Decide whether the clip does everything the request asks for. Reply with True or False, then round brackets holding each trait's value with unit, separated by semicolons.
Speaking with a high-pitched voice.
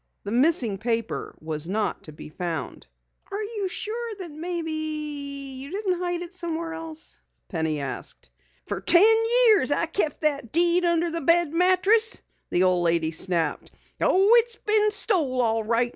True (315 Hz)